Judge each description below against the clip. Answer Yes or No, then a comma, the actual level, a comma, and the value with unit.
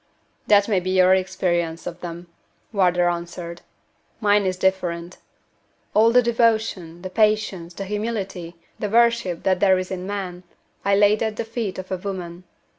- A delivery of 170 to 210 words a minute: No, average, 160 wpm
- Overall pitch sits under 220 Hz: Yes, high, 190 Hz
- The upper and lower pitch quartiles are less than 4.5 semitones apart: Yes, average, 2.9 semitones